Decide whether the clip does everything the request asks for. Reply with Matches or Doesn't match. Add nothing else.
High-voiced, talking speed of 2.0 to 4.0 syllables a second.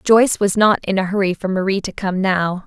Doesn't match